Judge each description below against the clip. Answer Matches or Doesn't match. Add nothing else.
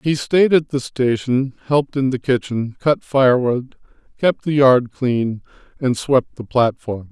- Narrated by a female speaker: Doesn't match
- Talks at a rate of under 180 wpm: Matches